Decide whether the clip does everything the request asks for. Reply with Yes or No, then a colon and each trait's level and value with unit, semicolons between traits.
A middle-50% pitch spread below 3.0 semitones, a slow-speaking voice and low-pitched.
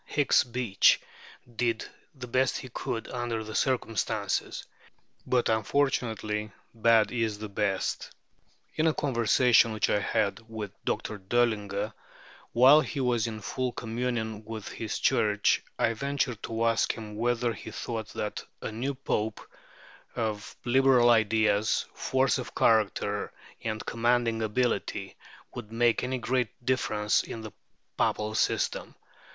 Yes: narrow, 2.4 semitones; slow, 130 wpm; low, 115 Hz